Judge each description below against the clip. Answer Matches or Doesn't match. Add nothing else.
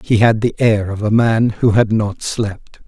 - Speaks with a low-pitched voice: Matches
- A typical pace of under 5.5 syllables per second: Matches